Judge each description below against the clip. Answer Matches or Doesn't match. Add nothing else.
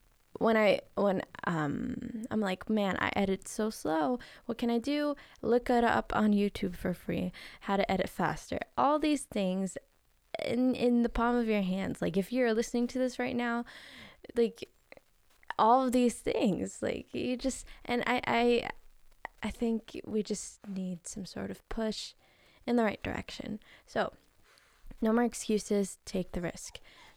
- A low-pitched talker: Doesn't match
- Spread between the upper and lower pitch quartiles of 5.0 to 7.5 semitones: Doesn't match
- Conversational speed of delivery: Matches